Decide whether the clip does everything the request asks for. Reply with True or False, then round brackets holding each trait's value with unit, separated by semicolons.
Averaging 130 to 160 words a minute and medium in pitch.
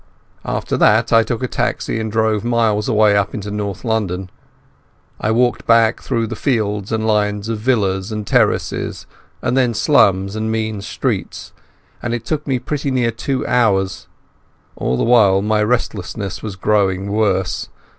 False (155 wpm; 110 Hz)